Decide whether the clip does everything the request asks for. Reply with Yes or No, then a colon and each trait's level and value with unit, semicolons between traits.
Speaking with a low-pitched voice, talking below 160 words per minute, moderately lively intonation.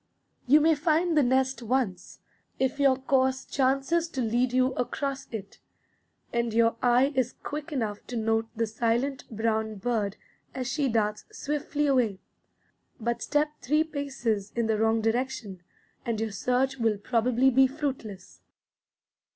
No: very high, 250 Hz; average, 145 wpm; average, 3.4 semitones